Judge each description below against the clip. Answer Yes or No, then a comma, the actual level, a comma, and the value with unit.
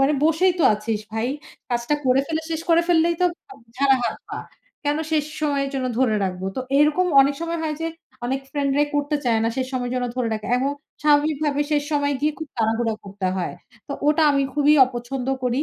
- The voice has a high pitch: Yes, very high, 280 Hz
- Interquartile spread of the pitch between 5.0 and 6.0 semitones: No, average, 3.8 semitones